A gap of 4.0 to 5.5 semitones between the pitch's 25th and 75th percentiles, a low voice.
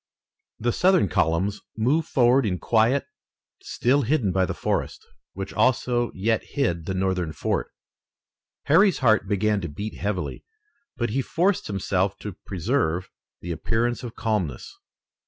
Yes: average, 5.0 semitones; low, 110 Hz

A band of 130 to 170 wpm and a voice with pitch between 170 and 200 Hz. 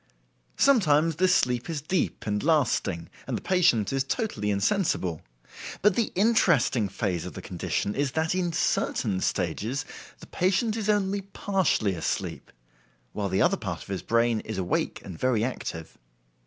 No: average, 155 wpm; low, 135 Hz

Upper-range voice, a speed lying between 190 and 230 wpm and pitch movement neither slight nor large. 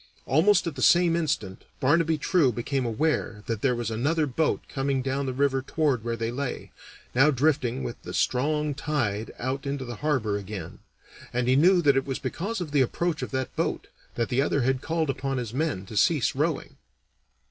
No: low, 135 Hz; average, 195 wpm; average, 4.0 semitones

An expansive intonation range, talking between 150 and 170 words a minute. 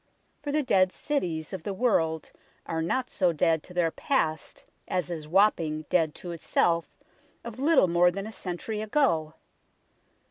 No: average, 4.8 semitones; average, 155 wpm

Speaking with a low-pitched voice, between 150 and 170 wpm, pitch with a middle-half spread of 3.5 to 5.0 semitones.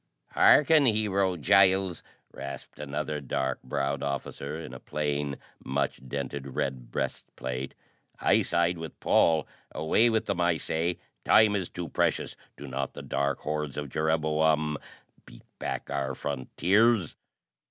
No: very low, 75 Hz; slow, 135 wpm; average, 4.2 semitones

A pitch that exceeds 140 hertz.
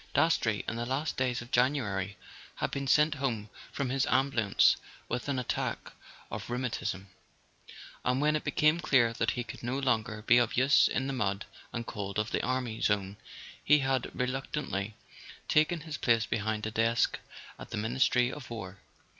No: low, 120 Hz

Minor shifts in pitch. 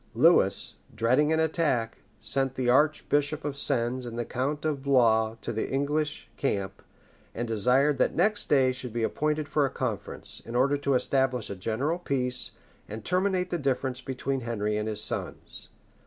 No: average, 3.9 semitones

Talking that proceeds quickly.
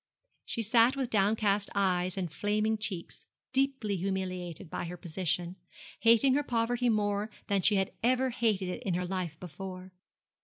No: average, 155 wpm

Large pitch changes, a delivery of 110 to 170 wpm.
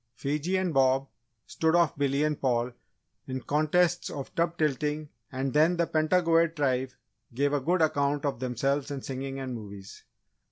No: average, 3.3 semitones; average, 160 wpm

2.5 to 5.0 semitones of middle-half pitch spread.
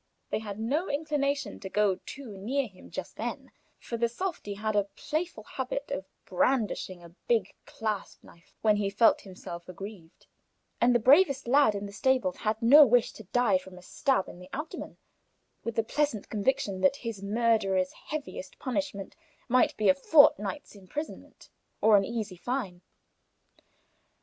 No: wide, 5.5 semitones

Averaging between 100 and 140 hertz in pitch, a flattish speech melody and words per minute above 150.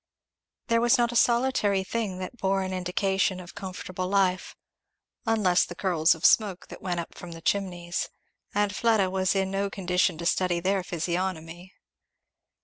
No: high, 190 Hz; narrow, 1.9 semitones; average, 160 wpm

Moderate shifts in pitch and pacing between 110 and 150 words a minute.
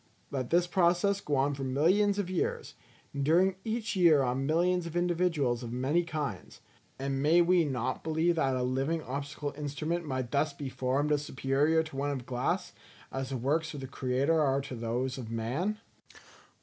No: average, 4.4 semitones; average, 185 wpm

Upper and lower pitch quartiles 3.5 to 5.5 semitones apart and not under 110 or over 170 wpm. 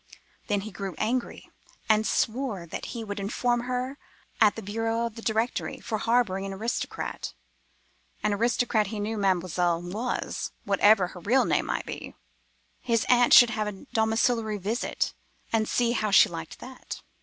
No: average, 2.9 semitones; average, 165 wpm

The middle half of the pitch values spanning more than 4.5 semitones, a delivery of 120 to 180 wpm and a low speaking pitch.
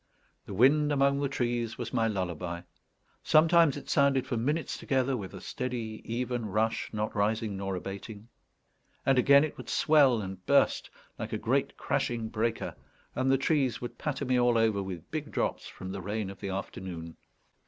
Yes: average, 5.1 semitones; average, 175 wpm; low, 115 Hz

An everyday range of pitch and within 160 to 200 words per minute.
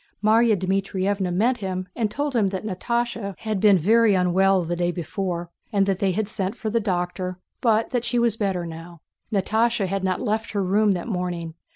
Yes: average, 3.2 semitones; average, 195 wpm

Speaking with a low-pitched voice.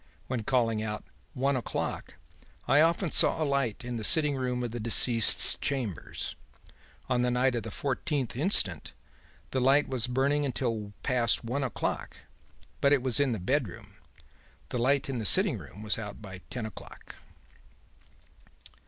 Yes: low, 125 Hz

